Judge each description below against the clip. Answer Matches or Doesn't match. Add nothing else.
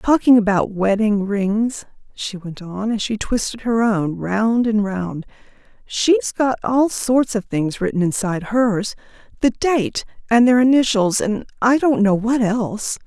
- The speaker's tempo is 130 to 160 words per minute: Matches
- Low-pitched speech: Doesn't match